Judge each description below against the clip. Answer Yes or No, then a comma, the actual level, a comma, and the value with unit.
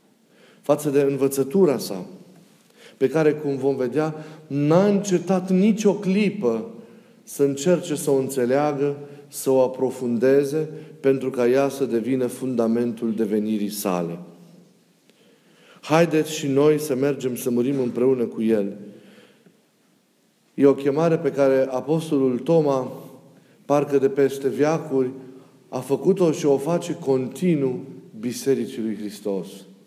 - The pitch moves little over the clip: No, average, 3.7 semitones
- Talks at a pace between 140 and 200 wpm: No, average, 120 wpm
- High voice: No, medium, 140 Hz